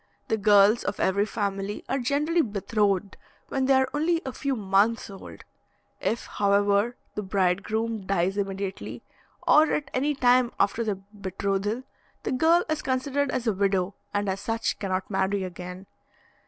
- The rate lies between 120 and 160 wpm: Yes, average, 155 wpm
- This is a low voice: No, high, 205 Hz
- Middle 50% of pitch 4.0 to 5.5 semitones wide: Yes, average, 4.6 semitones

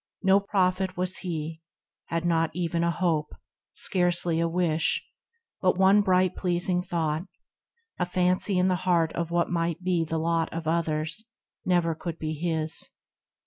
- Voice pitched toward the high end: No, medium, 175 Hz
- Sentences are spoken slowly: No, average, 155 wpm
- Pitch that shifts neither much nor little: No, narrow, 1.9 semitones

